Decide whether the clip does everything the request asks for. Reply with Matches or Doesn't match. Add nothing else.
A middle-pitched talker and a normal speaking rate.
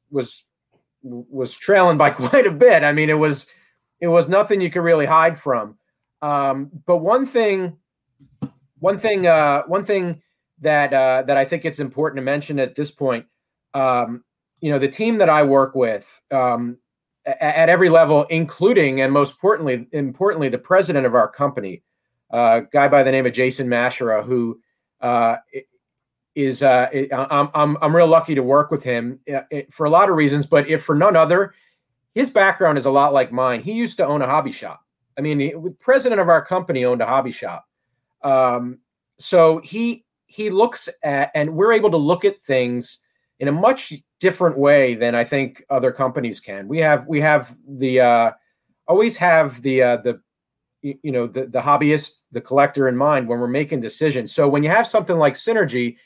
Matches